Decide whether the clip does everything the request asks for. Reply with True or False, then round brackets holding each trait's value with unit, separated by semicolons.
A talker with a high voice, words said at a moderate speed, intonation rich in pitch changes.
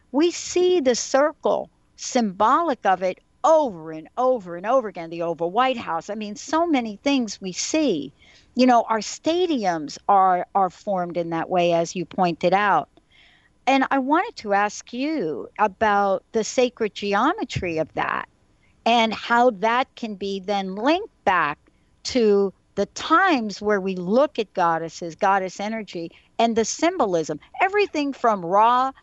True (220 Hz; 155 wpm; 6.0 semitones)